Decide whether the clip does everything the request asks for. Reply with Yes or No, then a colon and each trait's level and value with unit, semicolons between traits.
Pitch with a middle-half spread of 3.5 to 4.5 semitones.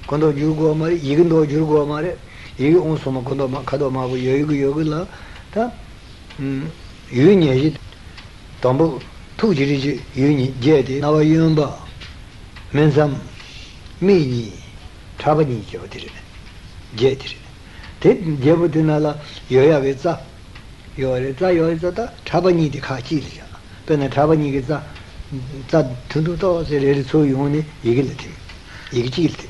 Yes: average, 3.9 semitones